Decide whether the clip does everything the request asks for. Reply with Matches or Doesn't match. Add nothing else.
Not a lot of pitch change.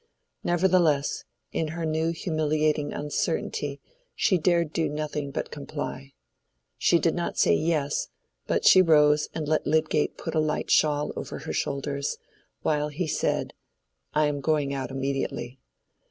Matches